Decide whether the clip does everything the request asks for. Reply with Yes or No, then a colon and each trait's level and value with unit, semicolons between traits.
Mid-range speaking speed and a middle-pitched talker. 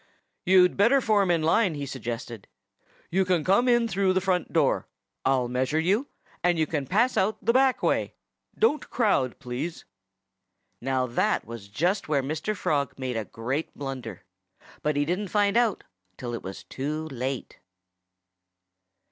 Yes: average, 160 wpm; medium, 160 Hz